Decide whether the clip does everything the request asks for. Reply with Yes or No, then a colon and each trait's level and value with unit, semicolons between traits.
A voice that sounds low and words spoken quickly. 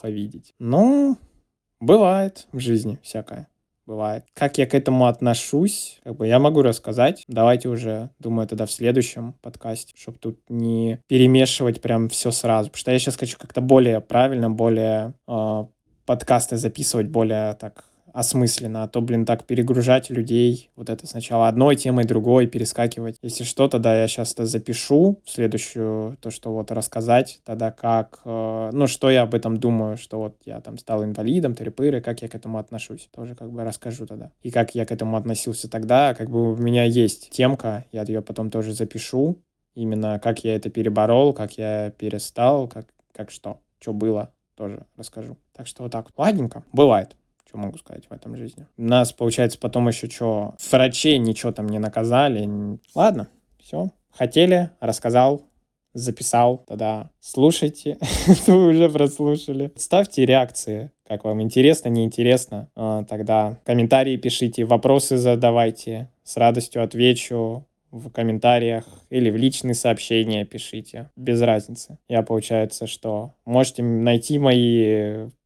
No: low, 115 Hz; average, 150 wpm